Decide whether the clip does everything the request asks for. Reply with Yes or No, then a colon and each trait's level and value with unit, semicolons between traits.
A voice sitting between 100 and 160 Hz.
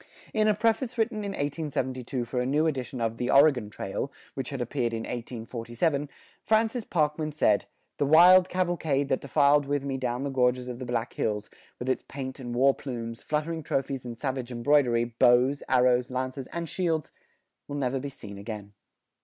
Yes: low, 135 Hz